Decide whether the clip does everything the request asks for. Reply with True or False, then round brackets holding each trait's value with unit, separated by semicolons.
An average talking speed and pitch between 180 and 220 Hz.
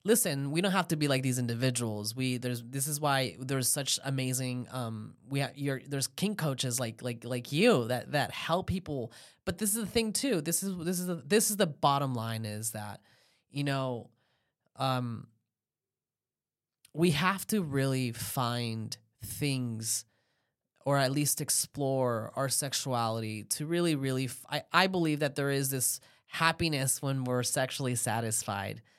False (170 wpm; 135 Hz)